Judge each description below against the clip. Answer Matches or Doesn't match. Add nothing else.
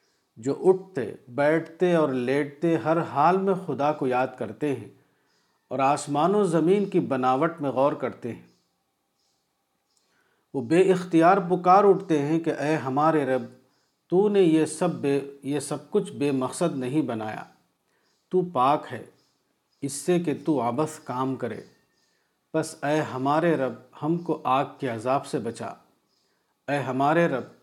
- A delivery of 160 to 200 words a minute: Doesn't match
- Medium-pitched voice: Matches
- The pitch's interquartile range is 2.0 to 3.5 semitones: Doesn't match